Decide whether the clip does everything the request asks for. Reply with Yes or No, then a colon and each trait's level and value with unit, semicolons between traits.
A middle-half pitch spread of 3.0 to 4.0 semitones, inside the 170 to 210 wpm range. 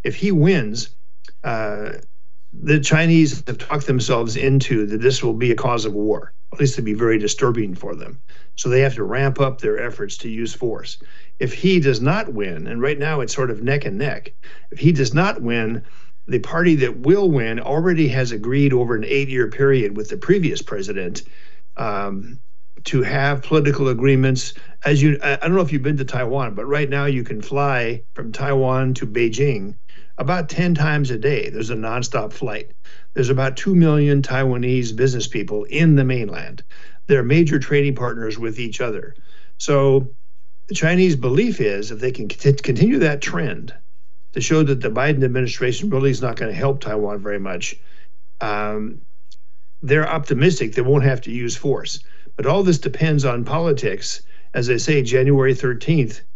Yes: average, 3.4 semitones; average, 180 wpm